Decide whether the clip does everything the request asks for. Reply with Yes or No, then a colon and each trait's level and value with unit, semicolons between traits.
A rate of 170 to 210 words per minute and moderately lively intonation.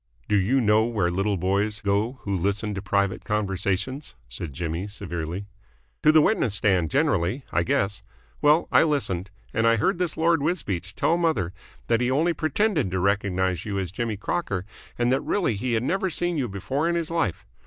No: average, 190 wpm; wide, 7.2 semitones